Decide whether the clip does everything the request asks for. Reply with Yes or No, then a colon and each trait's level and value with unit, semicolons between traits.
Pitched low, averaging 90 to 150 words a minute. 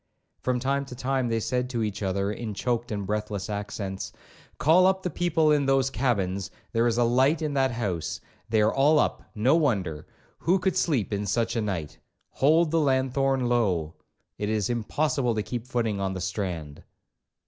No: low, 120 Hz; average, 165 wpm